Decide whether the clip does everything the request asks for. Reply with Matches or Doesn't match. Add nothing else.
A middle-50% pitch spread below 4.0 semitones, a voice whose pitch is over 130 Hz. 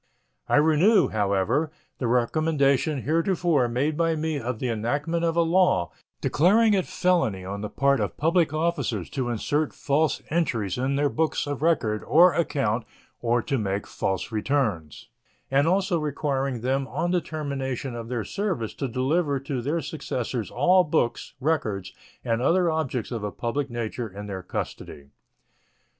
Doesn't match